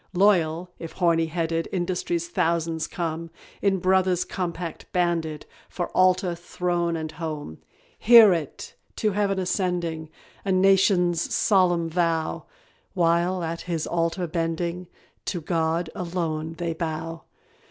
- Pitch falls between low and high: Yes, medium, 170 Hz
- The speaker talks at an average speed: No, slow, 120 wpm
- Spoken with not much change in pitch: Yes, narrow, 1.8 semitones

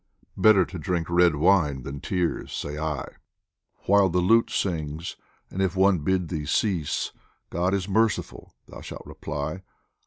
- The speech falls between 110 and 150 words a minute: No, average, 165 wpm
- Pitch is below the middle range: Yes, very low, 90 Hz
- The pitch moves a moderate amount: Yes, average, 3.7 semitones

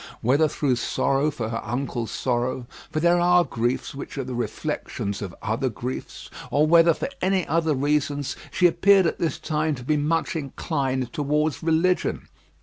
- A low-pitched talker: No, medium, 145 Hz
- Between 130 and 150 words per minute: No, average, 165 wpm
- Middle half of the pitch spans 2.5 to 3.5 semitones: No, average, 4.2 semitones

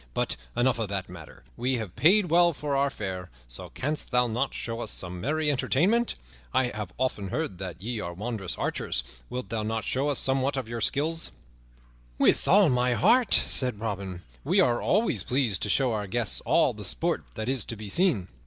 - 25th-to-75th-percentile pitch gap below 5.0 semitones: No, wide, 5.5 semitones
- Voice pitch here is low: Yes, low, 120 Hz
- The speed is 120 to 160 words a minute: No, average, 200 wpm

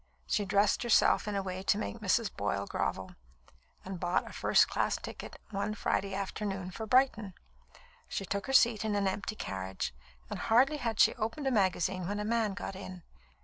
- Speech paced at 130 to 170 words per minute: No, average, 190 wpm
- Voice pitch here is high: Yes, high, 200 Hz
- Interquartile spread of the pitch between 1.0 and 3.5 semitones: Yes, average, 2.8 semitones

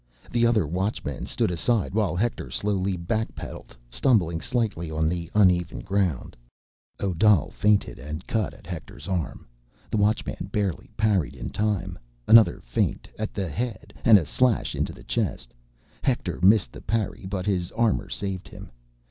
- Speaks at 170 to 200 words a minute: No, average, 150 wpm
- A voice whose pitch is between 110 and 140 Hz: No, very low, 95 Hz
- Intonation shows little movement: No, average, 4.0 semitones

